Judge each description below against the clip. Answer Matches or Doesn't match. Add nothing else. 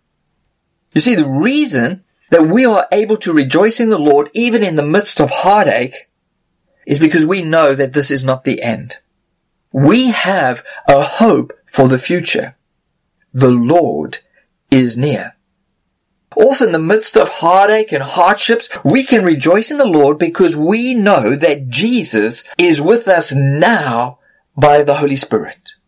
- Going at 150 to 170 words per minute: Matches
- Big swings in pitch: Matches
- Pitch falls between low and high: Matches